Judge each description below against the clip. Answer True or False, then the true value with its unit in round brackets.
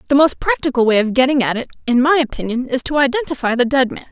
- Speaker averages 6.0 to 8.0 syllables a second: True (6.9 syllables/s)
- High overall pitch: True (265 Hz)